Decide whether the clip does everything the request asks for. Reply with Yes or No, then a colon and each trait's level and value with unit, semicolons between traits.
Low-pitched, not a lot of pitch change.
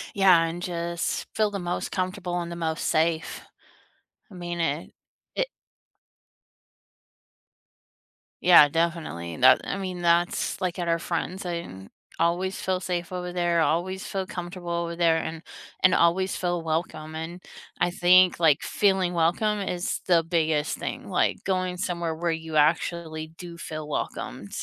No: medium, 170 Hz; narrow, 1.8 semitones